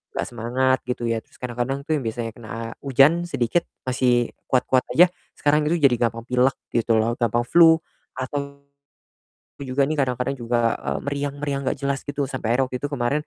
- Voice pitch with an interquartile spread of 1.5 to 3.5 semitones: Yes, average, 2.9 semitones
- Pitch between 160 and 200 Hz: No, low, 130 Hz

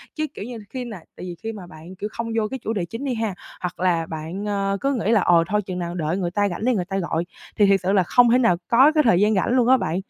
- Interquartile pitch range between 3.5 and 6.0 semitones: Yes, average, 4.6 semitones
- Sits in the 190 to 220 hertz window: Yes, high, 200 Hz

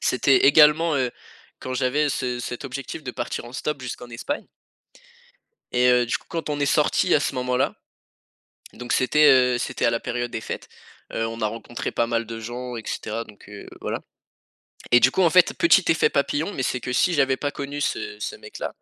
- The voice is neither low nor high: No, low, 125 Hz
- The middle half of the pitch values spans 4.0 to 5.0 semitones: No, average, 3.3 semitones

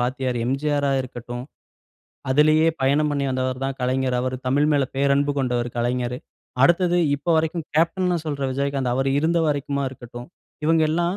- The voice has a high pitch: No, medium, 140 Hz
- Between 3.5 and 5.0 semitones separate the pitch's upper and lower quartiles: No, average, 3.0 semitones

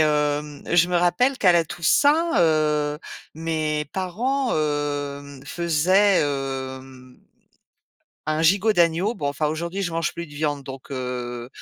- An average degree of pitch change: Yes, average, 3.5 semitones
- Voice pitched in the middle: Yes, medium, 155 Hz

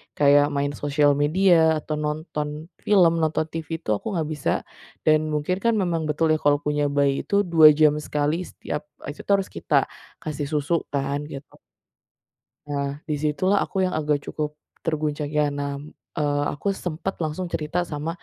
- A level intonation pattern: Yes, narrow, 2.2 semitones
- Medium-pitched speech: Yes, medium, 150 Hz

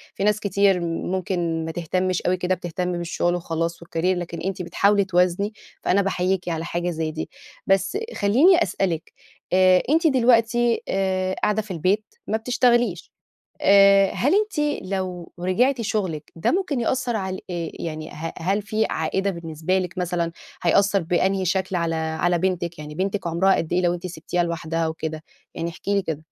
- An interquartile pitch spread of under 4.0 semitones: Yes, average, 3.0 semitones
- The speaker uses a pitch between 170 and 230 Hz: Yes, medium, 185 Hz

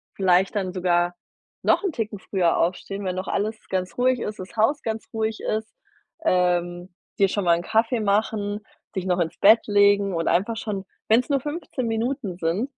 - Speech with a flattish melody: No, average, 3.5 semitones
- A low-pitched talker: No, high, 200 Hz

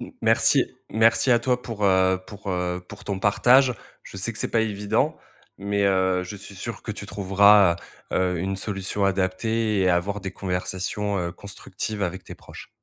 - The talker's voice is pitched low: Yes, low, 100 Hz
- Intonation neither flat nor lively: No, narrow, 2.1 semitones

